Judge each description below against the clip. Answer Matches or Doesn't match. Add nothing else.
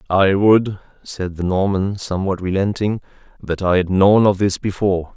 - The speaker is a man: Matches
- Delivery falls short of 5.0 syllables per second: Matches